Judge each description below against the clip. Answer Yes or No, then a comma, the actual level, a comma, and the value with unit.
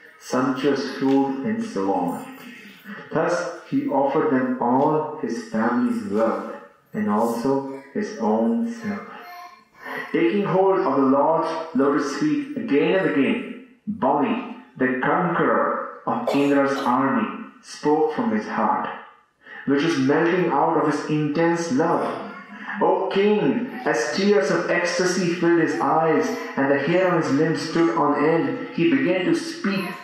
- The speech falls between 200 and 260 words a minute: No, slow, 135 wpm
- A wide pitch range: Yes, wide, 7.2 semitones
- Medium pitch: Yes, medium, 175 Hz